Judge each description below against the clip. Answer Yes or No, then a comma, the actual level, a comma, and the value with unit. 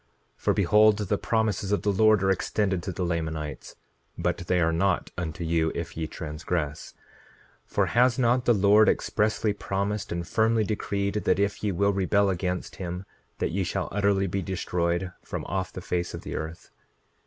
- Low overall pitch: Yes, very low, 95 Hz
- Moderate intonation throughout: Yes, average, 3.2 semitones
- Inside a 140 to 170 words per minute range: No, average, 180 wpm